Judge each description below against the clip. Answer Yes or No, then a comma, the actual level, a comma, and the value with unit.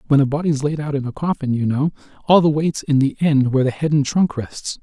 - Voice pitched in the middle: Yes, medium, 145 Hz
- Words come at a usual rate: No, fast, 275 wpm